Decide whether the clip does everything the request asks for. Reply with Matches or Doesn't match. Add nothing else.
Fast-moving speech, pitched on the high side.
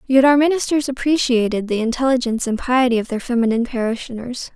Doesn't match